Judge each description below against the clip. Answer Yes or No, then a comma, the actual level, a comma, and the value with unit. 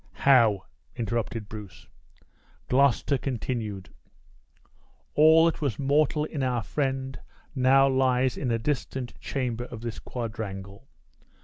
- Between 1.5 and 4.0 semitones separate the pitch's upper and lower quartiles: Yes, average, 3.3 semitones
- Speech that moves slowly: Yes, slow, 110 wpm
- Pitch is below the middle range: Yes, low, 125 Hz